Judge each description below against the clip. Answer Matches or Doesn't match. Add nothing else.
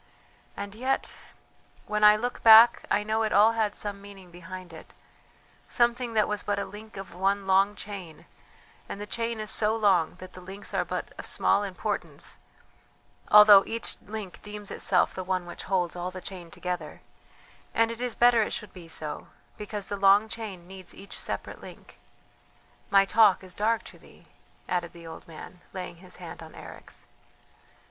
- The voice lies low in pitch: Doesn't match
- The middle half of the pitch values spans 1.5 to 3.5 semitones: Matches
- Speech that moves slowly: Doesn't match